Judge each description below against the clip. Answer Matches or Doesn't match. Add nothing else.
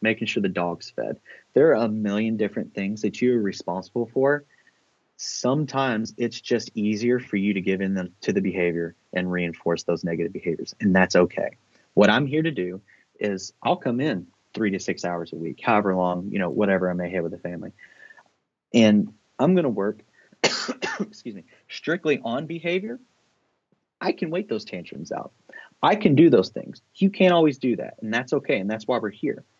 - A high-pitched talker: Doesn't match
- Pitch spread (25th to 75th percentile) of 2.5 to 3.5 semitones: Doesn't match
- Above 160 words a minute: Matches